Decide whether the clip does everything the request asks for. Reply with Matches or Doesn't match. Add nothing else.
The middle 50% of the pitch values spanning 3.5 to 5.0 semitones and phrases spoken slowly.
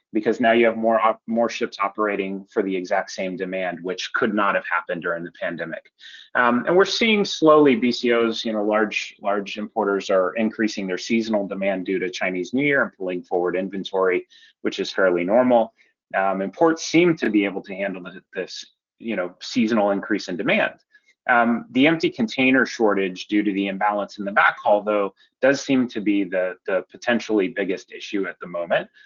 Doesn't match